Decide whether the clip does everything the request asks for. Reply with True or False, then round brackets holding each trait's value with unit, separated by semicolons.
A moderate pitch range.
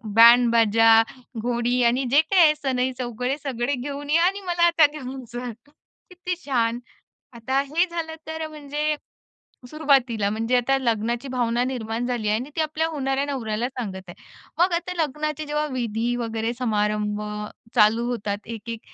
True (4.5 semitones)